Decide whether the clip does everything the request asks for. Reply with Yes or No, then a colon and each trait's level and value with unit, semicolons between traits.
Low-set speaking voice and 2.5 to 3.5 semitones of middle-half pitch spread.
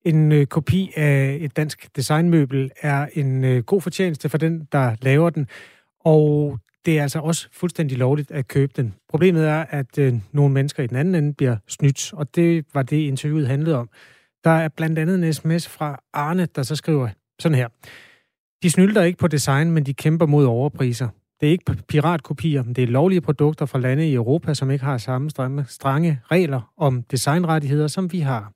No: medium, 150 Hz; average, 3.1 semitones